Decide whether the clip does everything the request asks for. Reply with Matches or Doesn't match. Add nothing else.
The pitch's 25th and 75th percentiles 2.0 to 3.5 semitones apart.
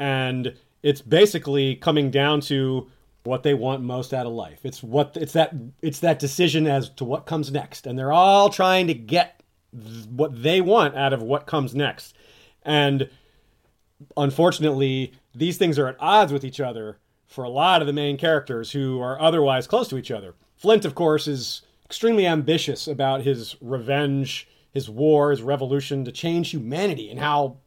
Matches